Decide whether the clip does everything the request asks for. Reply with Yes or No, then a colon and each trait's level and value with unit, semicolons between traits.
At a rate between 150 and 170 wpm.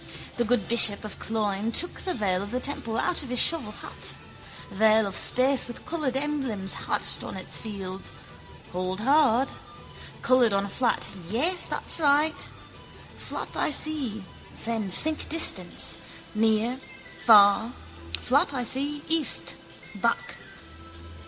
No: slow, 135 wpm